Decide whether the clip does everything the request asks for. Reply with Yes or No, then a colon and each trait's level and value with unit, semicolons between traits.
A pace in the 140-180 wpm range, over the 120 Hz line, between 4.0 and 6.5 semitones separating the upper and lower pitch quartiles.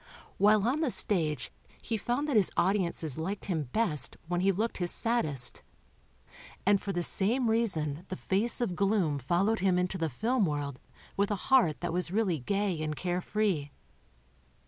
Yes: average, 170 wpm; high, 190 Hz; average, 4.9 semitones